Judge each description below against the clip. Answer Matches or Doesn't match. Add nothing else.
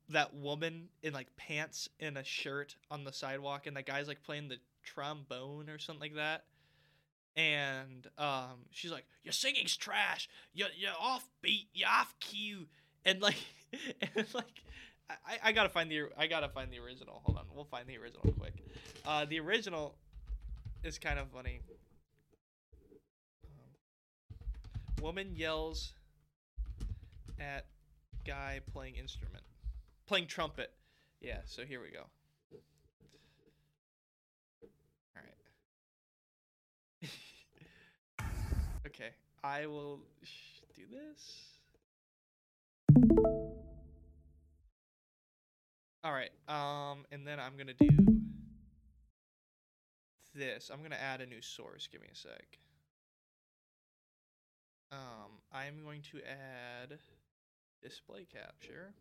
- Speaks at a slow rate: Matches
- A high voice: Doesn't match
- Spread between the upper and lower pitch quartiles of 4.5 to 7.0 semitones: Doesn't match